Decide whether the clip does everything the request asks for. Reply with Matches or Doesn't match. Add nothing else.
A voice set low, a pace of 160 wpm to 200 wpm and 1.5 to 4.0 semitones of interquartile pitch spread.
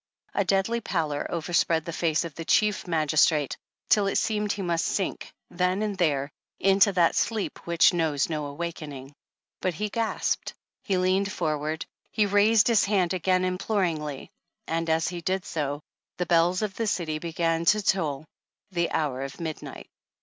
Doesn't match